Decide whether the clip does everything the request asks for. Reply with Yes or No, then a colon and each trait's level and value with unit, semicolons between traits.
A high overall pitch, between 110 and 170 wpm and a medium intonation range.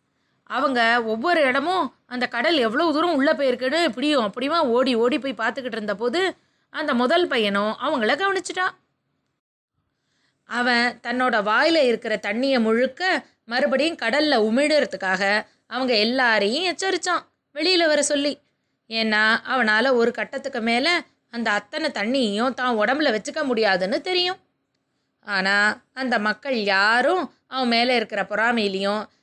Yes: very high, 250 Hz; average, 120 wpm; average, 5.0 semitones